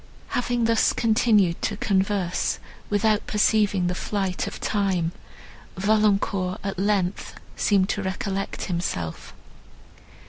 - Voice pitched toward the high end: Yes, high, 200 Hz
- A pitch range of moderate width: No, narrow, 2.3 semitones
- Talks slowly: Yes, slow, 105 wpm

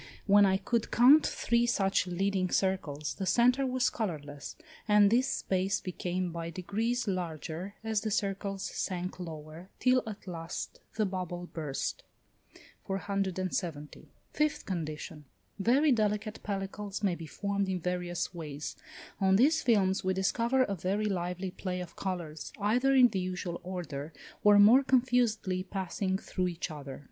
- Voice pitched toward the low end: No, high, 190 Hz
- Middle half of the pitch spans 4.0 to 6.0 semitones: No, average, 3.2 semitones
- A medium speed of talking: Yes, average, 145 wpm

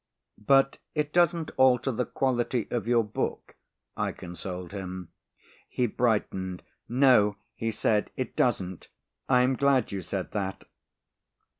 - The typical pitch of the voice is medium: No, low, 120 Hz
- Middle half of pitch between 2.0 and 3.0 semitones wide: No, average, 5.1 semitones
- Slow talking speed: Yes, slow, 130 wpm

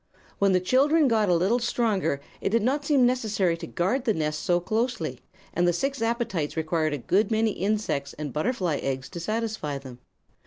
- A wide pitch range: Yes, wide, 6.5 semitones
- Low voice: No, high, 200 Hz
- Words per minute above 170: Yes, average, 190 wpm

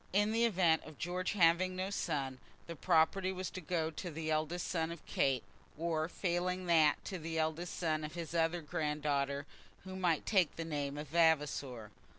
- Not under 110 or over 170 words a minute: No, average, 180 wpm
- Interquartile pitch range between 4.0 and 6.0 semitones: No, average, 2.8 semitones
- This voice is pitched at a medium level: Yes, medium, 165 Hz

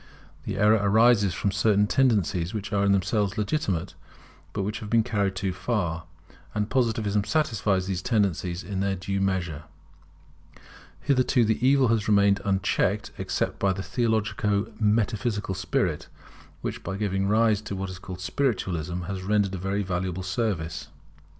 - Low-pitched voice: Yes, low, 100 Hz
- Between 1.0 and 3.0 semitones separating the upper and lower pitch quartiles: Yes, narrow, 2.5 semitones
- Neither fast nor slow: Yes, average, 150 wpm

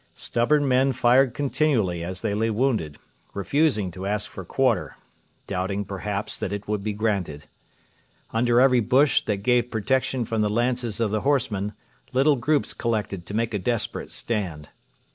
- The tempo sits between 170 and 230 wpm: No, average, 160 wpm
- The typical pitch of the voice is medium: No, low, 110 Hz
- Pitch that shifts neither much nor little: Yes, average, 4.0 semitones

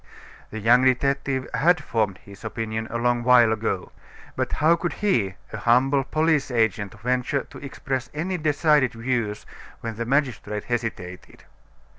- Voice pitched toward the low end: Yes, low, 120 Hz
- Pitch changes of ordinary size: Yes, average, 3.9 semitones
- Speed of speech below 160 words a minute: Yes, average, 145 wpm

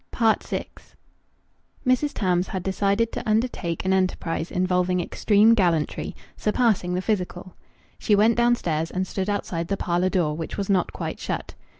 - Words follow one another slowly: No, average, 150 wpm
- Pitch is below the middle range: No, high, 190 Hz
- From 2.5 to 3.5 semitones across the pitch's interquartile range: Yes, average, 3.2 semitones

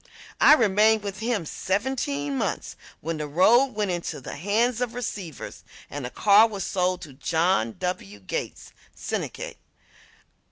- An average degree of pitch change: No, wide, 6.2 semitones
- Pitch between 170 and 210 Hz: Yes, high, 190 Hz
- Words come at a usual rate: Yes, average, 145 wpm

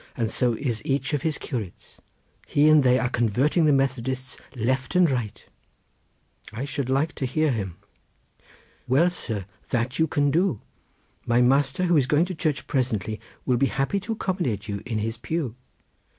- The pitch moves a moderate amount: Yes, average, 4.3 semitones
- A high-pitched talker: No, low, 130 Hz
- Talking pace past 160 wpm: Yes, average, 170 wpm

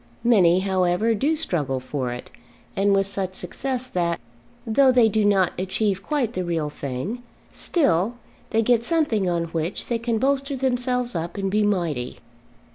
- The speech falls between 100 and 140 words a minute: No, average, 160 wpm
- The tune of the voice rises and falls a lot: Yes, wide, 5.9 semitones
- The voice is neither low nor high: No, high, 200 Hz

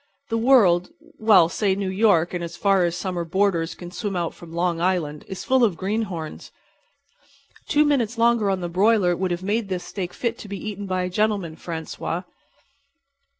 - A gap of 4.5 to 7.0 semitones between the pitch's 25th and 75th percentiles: No, average, 3.7 semitones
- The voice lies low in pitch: No, high, 190 Hz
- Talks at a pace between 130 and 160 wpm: No, average, 175 wpm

